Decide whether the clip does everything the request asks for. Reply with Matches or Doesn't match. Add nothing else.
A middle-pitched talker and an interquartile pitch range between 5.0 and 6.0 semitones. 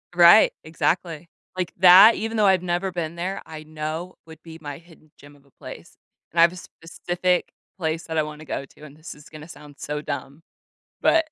Doesn't match